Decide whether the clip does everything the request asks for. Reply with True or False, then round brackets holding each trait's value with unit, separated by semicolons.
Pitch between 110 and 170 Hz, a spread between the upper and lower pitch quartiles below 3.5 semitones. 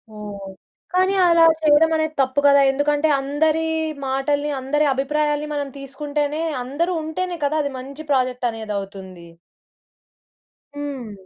False (290 Hz; 2.9 semitones)